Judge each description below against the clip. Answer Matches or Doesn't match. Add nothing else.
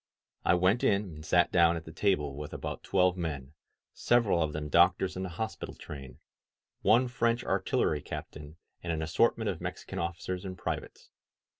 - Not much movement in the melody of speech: Doesn't match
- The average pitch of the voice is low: Matches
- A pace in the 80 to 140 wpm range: Doesn't match